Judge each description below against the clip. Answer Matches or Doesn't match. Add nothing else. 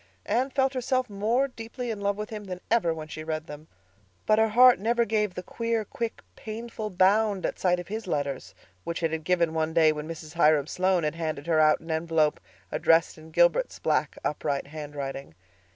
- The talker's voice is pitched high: Doesn't match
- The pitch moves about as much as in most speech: Doesn't match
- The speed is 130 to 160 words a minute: Doesn't match